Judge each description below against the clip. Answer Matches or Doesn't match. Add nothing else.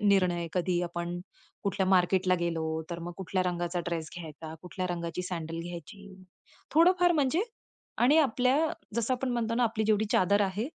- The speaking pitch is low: Doesn't match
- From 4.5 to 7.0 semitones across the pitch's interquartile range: Matches